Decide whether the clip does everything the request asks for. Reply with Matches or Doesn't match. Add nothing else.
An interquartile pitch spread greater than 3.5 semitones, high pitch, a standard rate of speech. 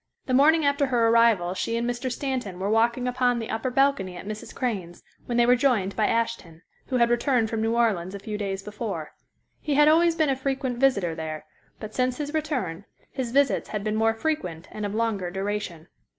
Doesn't match